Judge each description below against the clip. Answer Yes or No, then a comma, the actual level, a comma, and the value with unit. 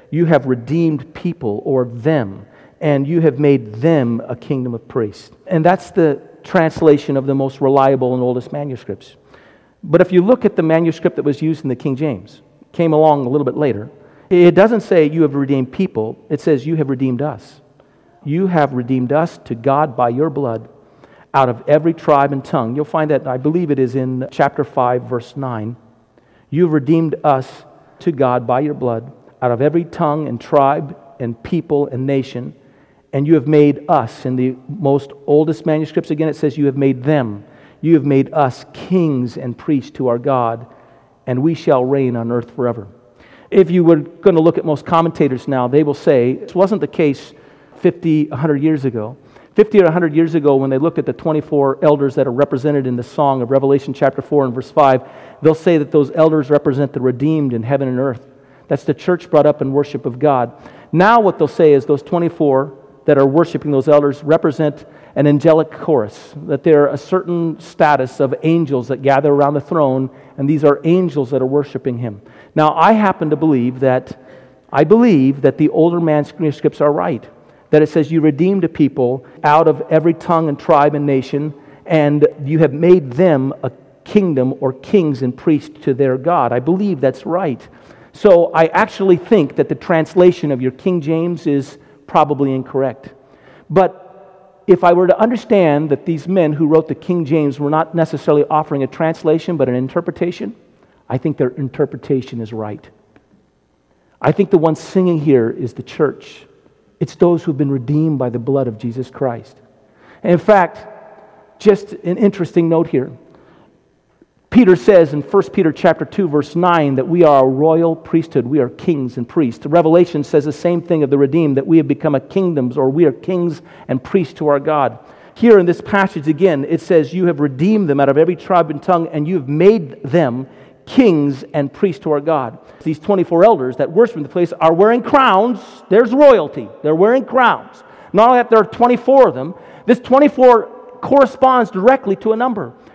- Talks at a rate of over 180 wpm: Yes, average, 195 wpm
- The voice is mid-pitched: Yes, medium, 150 Hz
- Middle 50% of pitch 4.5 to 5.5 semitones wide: No, average, 3.9 semitones